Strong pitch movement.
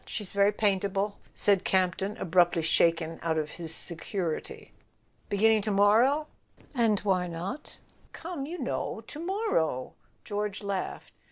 No: average, 3.9 semitones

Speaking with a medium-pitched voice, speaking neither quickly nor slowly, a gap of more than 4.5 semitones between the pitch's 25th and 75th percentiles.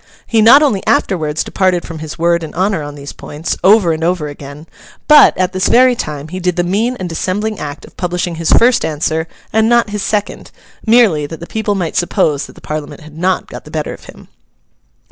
No: medium, 175 Hz; fast, 210 wpm; average, 4.9 semitones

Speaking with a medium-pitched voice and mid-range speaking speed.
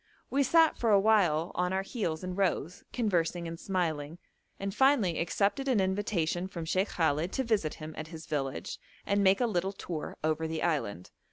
Yes: medium, 180 Hz; average, 180 wpm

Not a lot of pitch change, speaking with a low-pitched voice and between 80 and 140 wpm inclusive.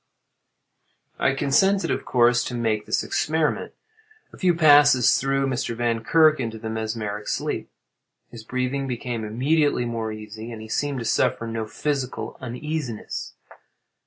No: average, 4.1 semitones; low, 125 Hz; slow, 135 wpm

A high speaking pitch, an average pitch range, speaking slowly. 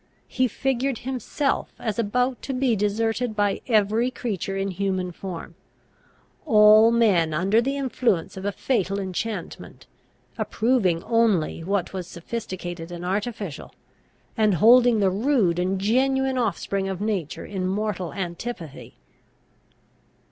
Yes: high, 210 Hz; average, 4.1 semitones; slow, 125 wpm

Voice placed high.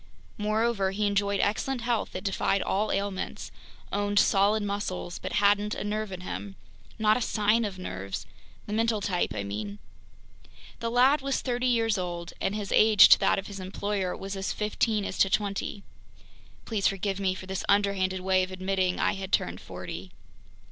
Yes: high, 200 Hz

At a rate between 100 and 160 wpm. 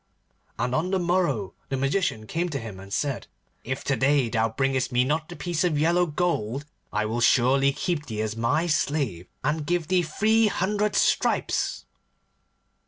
No: average, 170 wpm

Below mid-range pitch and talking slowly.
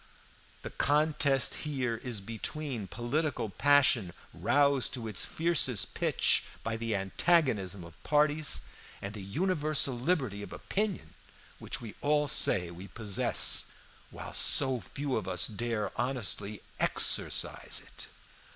Yes: low, 125 Hz; slow, 125 wpm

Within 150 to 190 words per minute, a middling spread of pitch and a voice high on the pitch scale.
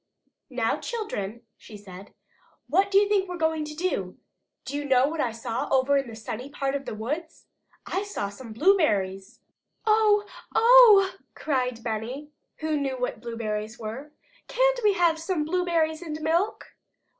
No: average, 160 wpm; wide, 7.9 semitones; very high, 295 Hz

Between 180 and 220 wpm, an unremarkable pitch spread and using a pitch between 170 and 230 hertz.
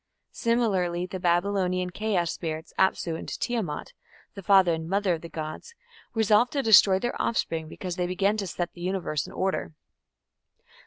No: average, 160 wpm; average, 3.0 semitones; medium, 185 Hz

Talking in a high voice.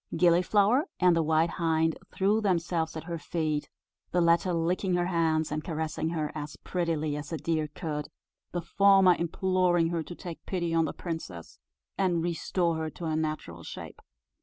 No: medium, 165 Hz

